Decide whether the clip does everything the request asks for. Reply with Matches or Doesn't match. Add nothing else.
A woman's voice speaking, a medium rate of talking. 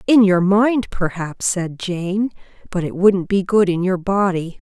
Matches